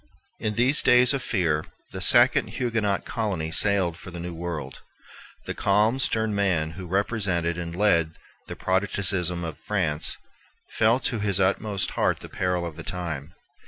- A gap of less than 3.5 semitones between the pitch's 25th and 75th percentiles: No, average, 3.8 semitones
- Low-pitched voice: Yes, very low, 95 Hz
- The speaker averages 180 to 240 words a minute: No, average, 160 wpm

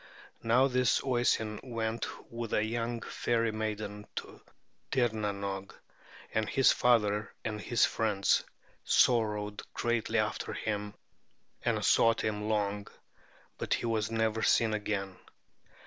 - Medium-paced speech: No, slow, 115 wpm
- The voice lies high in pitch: No, low, 110 Hz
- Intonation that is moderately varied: No, narrow, 1.9 semitones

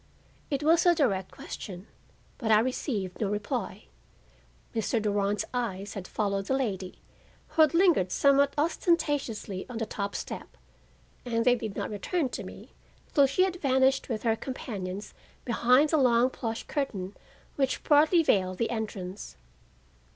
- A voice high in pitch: Yes, high, 235 Hz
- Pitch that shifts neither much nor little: No, wide, 5.7 semitones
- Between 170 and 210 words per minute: No, average, 150 wpm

